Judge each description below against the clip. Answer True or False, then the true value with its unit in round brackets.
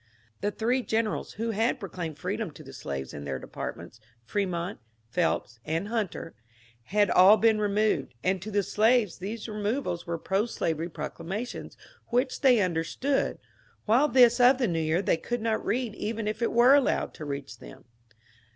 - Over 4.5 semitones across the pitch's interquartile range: True (5.5 semitones)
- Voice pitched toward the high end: True (205 Hz)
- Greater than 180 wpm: False (175 wpm)